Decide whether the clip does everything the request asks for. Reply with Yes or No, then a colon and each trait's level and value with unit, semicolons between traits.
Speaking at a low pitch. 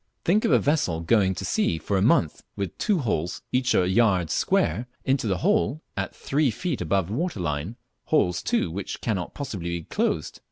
Yes: low, 100 Hz